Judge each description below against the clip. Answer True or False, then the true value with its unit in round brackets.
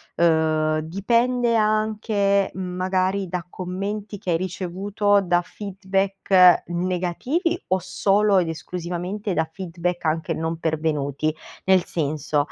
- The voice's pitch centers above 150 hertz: True (185 Hz)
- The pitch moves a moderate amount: True (3.0 semitones)